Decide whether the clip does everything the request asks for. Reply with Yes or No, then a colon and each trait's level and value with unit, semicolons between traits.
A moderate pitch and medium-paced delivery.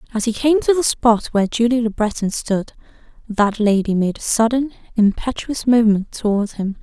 No: high, 225 Hz; average, 175 wpm